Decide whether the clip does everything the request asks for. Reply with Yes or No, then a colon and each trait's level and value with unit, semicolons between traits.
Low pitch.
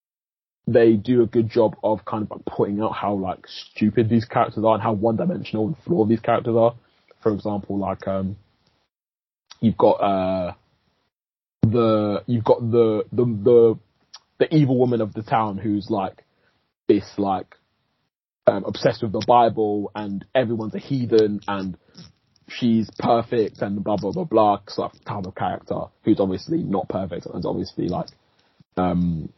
Yes: low, 110 Hz